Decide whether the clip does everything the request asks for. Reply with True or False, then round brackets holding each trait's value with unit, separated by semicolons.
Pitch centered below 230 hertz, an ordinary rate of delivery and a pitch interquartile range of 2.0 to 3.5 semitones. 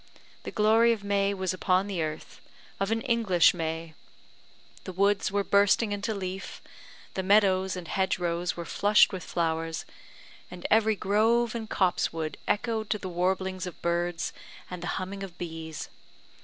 True (190 Hz; 155 wpm; 2.8 semitones)